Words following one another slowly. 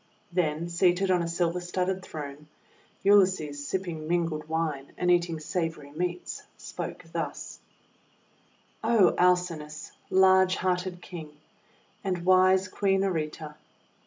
Yes: slow, 110 wpm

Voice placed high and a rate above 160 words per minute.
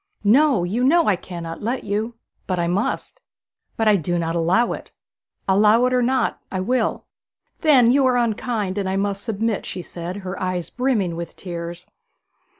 Yes: high, 205 Hz; average, 175 wpm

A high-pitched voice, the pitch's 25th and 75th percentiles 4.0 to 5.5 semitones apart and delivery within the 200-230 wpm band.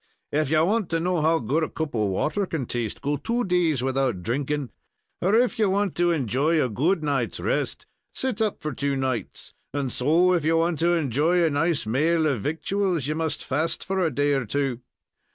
No: medium, 155 Hz; average, 4.4 semitones; fast, 205 wpm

